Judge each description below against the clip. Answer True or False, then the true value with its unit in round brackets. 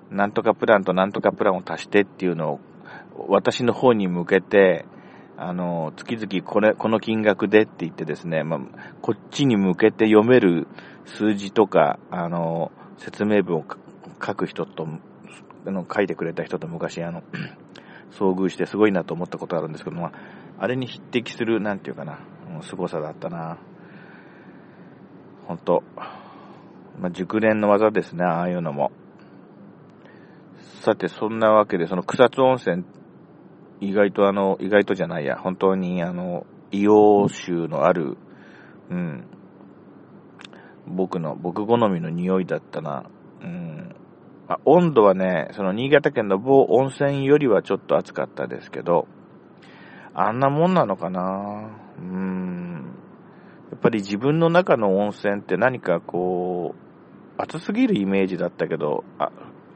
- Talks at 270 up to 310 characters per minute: True (275 characters per minute)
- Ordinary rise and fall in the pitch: True (3.7 semitones)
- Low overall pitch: True (100 Hz)